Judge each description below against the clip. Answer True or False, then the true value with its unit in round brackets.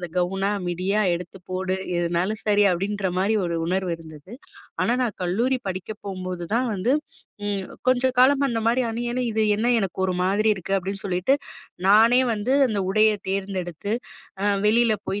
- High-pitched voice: True (200 Hz)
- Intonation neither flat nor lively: True (3.3 semitones)